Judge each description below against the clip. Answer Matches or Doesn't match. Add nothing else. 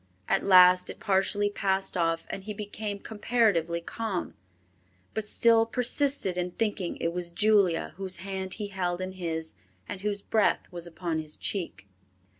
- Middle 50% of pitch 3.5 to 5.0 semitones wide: Doesn't match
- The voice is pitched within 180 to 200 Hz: Matches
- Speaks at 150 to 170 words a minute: Matches